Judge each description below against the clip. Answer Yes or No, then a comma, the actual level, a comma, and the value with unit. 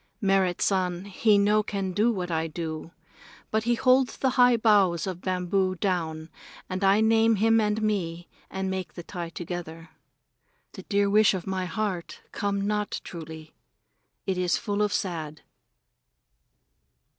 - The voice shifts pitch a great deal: No, average, 3.2 semitones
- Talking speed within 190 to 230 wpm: No, average, 150 wpm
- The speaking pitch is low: No, high, 190 Hz